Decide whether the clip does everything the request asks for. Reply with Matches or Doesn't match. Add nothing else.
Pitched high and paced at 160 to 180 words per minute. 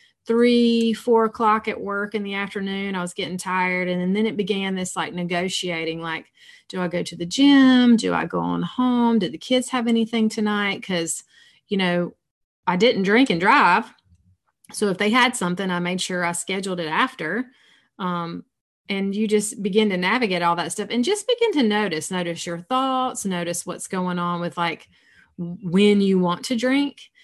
Doesn't match